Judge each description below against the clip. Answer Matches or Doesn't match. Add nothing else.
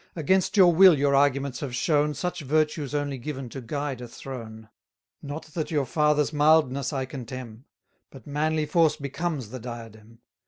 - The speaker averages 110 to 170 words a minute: Matches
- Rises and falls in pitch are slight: Doesn't match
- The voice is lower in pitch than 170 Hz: Matches